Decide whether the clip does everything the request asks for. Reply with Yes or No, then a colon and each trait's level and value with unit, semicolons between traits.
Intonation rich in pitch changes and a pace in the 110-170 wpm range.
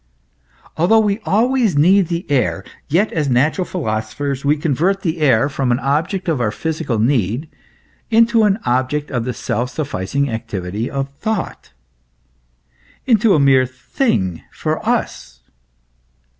Yes: wide, 7.1 semitones; average, 145 wpm